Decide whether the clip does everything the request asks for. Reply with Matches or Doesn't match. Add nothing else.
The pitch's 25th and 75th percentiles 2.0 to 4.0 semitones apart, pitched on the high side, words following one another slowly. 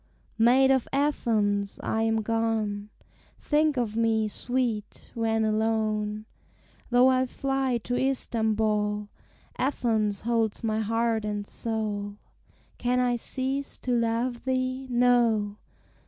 Matches